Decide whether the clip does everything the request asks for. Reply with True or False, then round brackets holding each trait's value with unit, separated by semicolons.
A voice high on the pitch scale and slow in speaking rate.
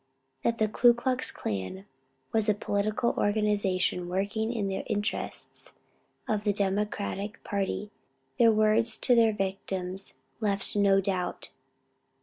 True (205 Hz; 125 wpm)